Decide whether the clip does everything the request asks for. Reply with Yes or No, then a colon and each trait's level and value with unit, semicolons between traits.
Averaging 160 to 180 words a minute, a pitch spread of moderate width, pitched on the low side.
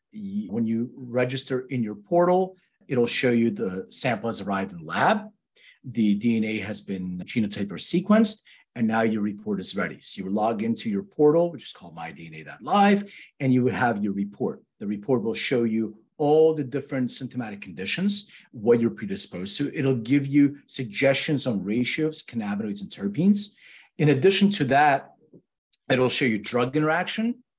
No: average, 170 wpm; wide, 8.5 semitones; low, 130 Hz